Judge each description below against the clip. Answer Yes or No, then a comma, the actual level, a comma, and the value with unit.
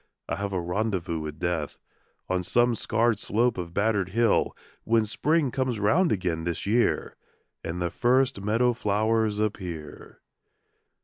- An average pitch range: Yes, average, 4.6 semitones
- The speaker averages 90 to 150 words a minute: Yes, average, 140 wpm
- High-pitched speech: No, low, 105 Hz